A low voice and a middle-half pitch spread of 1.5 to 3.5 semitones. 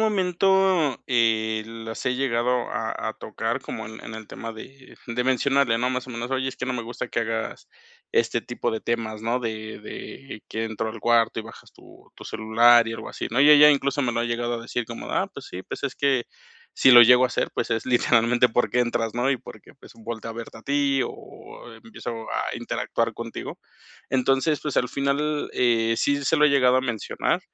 Yes: low, 120 Hz; average, 2.7 semitones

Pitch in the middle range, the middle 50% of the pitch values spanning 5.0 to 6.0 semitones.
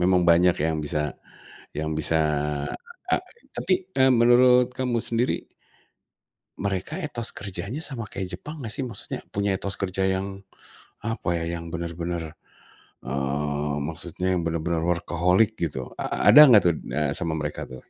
No: very low, 90 Hz; wide, 5.6 semitones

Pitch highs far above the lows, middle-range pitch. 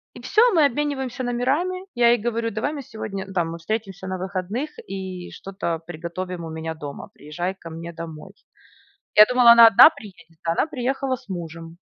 No: wide, 6.3 semitones; high, 195 Hz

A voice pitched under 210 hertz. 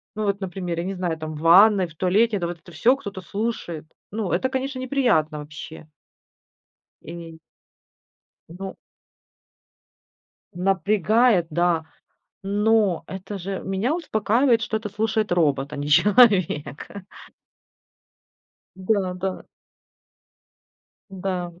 Yes: high, 190 Hz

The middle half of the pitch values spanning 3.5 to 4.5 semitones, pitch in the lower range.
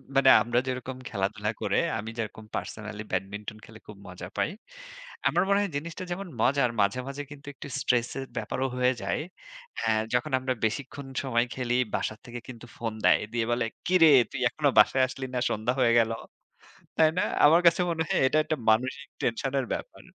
Yes: average, 4.1 semitones; low, 125 Hz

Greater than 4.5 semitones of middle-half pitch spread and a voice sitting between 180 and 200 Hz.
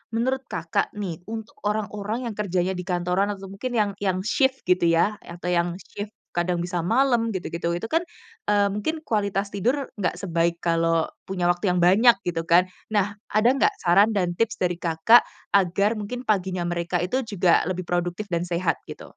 No: average, 3.5 semitones; high, 190 Hz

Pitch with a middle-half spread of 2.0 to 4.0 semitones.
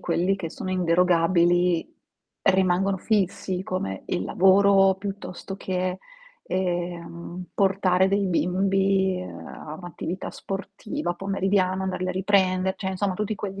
No: narrow, 1.4 semitones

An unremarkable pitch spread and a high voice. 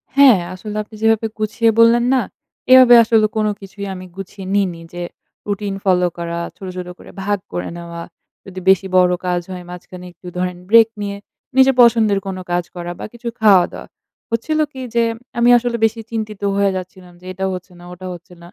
Yes: average, 3.8 semitones; high, 200 Hz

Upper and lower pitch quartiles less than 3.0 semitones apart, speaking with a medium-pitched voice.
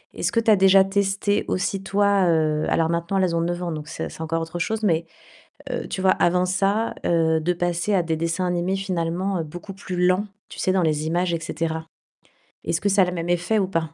Yes: narrow, 2.6 semitones; medium, 175 Hz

